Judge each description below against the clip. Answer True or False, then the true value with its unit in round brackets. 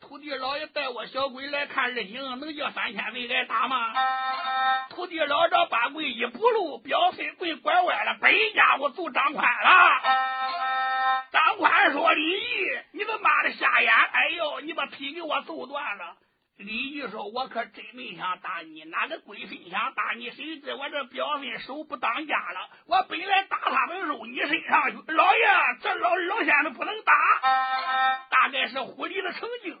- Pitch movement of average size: True (5.0 semitones)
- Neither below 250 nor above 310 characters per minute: False (240 characters per minute)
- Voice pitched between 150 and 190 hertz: False (290 Hz)